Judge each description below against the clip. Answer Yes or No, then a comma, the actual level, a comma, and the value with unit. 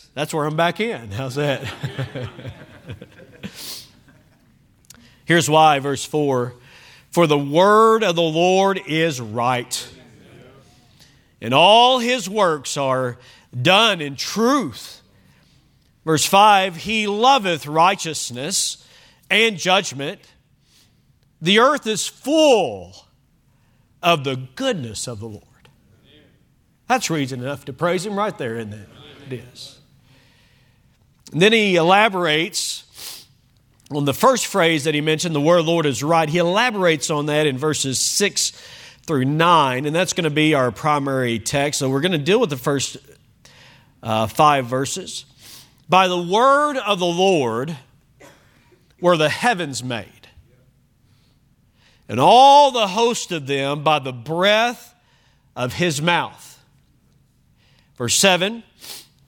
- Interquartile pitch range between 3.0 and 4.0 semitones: No, average, 5.2 semitones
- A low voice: No, medium, 145 Hz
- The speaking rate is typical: No, slow, 130 wpm